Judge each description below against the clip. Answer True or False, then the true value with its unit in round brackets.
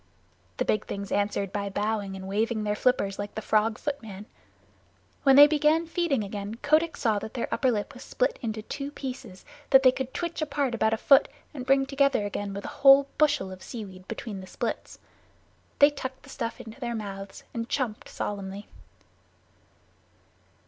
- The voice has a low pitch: False (230 Hz)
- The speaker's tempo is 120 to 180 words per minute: True (175 wpm)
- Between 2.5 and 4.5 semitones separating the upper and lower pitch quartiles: False (5.2 semitones)